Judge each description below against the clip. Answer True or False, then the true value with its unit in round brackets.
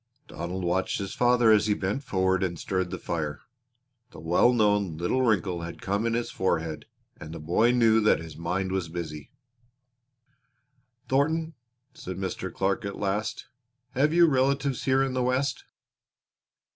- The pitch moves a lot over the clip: True (6.0 semitones)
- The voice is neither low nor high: False (100 Hz)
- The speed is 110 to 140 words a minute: False (160 wpm)